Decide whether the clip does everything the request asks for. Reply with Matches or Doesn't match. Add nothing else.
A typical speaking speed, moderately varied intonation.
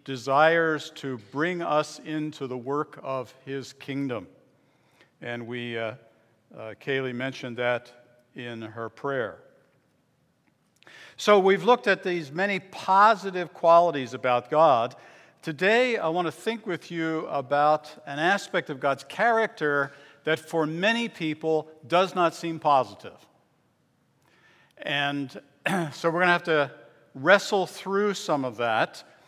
Doesn't match